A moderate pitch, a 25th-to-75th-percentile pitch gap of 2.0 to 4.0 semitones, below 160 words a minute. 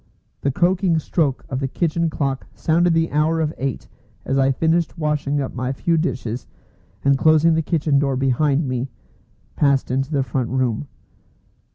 No: medium, 145 Hz; average, 3.4 semitones; average, 165 wpm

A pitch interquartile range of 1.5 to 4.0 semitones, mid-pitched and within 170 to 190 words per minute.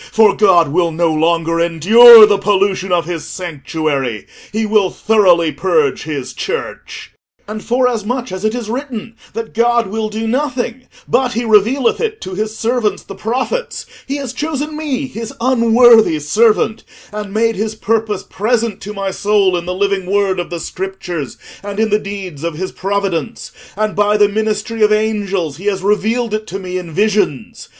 No: average, 3.6 semitones; high, 210 Hz; average, 175 wpm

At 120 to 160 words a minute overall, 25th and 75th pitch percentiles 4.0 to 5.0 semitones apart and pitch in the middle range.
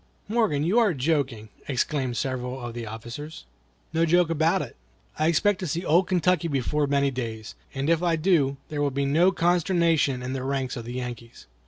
No: average, 185 wpm; average, 4.7 semitones; medium, 145 Hz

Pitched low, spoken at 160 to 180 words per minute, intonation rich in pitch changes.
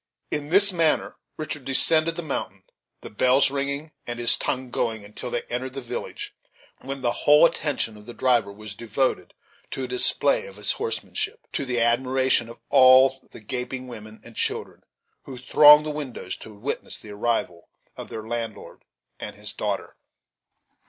No: low, 130 Hz; average, 165 wpm; average, 3.8 semitones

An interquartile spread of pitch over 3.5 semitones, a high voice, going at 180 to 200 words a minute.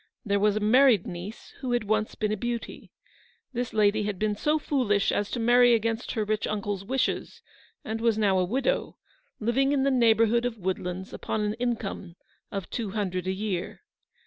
No: average, 3.0 semitones; high, 215 Hz; average, 185 wpm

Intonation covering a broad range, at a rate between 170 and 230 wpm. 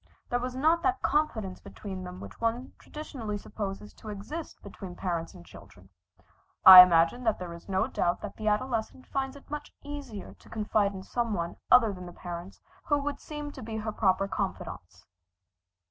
Yes: wide, 5.7 semitones; average, 180 wpm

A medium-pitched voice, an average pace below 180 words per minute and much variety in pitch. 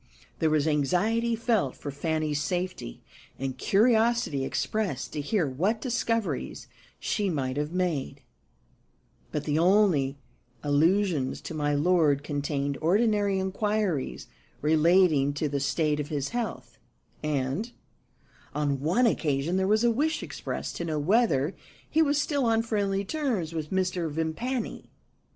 Yes: medium, 170 Hz; slow, 135 wpm; wide, 6.6 semitones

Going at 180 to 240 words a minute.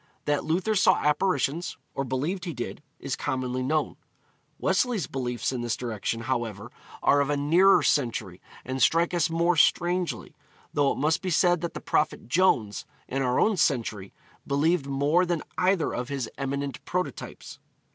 No: average, 160 wpm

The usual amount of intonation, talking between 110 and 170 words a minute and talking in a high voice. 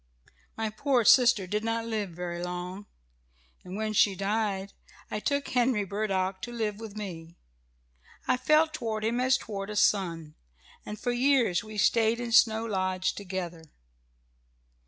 Yes: average, 3.4 semitones; average, 150 wpm; high, 210 Hz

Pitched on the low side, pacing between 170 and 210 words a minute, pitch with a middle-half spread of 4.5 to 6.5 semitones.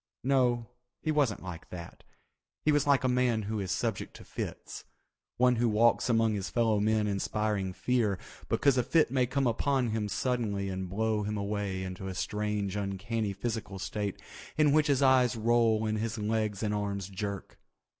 No: low, 110 Hz; average, 175 wpm; average, 3.4 semitones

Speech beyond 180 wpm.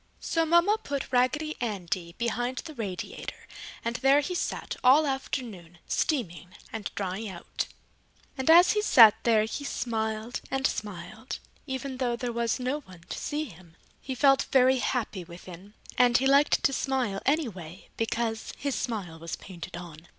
No: average, 160 wpm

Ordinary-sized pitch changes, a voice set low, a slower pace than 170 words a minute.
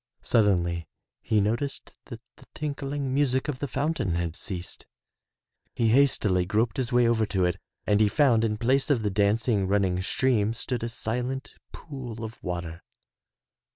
Yes: average, 4.6 semitones; low, 115 Hz; average, 155 wpm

